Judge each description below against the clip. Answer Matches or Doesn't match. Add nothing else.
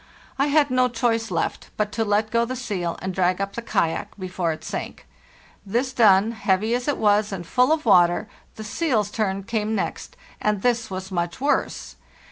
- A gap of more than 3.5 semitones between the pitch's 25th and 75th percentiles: Matches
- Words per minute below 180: Doesn't match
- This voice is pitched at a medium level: Doesn't match